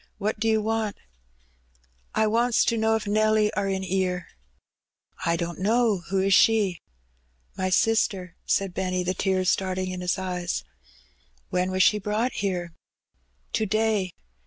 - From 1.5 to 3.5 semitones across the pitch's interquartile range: Yes, average, 2.8 semitones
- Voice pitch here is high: Yes, high, 195 Hz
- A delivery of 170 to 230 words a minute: No, average, 160 wpm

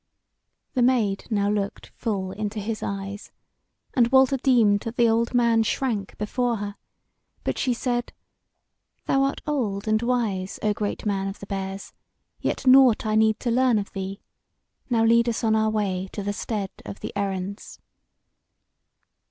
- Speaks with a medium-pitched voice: No, high, 215 Hz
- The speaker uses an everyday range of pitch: Yes, average, 3.1 semitones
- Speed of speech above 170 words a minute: No, average, 160 wpm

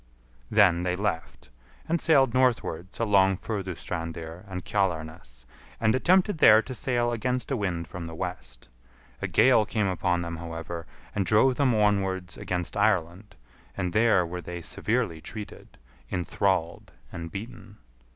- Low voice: Yes, very low, 95 Hz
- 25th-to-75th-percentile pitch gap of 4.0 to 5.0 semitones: Yes, average, 4.6 semitones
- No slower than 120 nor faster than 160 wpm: Yes, average, 140 wpm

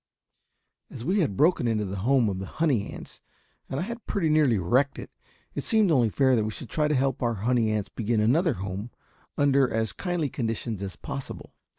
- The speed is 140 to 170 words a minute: No, average, 200 wpm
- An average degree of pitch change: No, wide, 5.7 semitones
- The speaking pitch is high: No, low, 125 Hz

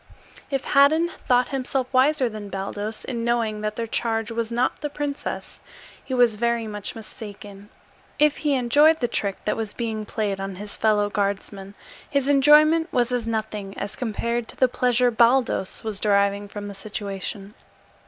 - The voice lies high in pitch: Yes, high, 230 Hz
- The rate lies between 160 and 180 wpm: Yes, average, 165 wpm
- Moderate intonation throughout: Yes, average, 3.7 semitones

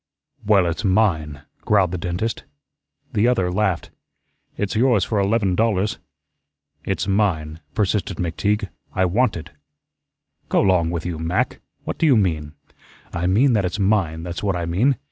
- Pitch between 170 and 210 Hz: No, very low, 95 Hz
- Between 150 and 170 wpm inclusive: Yes, average, 155 wpm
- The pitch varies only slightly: No, average, 3.6 semitones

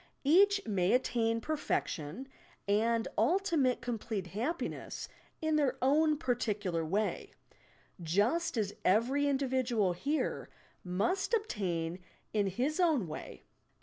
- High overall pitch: Yes, high, 235 Hz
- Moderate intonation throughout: No, wide, 6.7 semitones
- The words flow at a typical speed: No, slow, 115 wpm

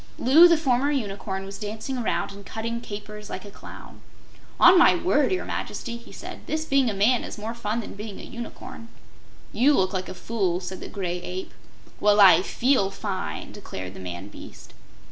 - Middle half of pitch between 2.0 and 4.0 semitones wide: No, average, 4.4 semitones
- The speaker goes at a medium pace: Yes, average, 190 wpm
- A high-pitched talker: Yes, high, 210 Hz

